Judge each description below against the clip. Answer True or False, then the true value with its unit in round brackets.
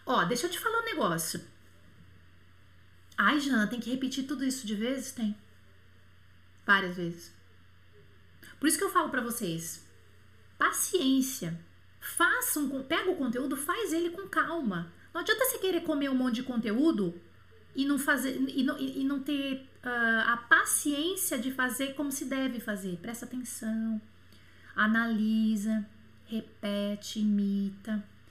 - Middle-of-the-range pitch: False (235 Hz)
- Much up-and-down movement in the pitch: True (8.0 semitones)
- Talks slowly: True (140 wpm)